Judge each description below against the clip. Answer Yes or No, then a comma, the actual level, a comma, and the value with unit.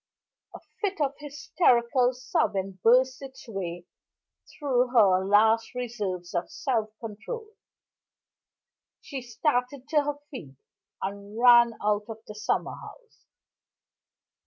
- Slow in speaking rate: Yes, slow, 110 wpm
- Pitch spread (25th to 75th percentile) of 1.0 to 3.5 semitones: No, average, 4.5 semitones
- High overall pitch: Yes, high, 240 Hz